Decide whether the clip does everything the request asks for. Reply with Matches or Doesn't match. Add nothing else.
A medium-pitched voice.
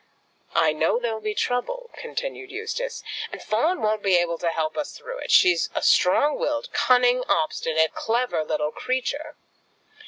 Doesn't match